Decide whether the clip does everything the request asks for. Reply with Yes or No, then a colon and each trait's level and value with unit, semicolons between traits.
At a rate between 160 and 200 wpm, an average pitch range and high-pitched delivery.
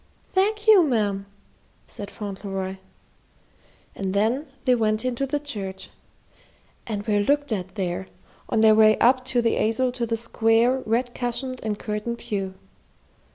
No: average, 140 wpm; average, 3.8 semitones; high, 225 Hz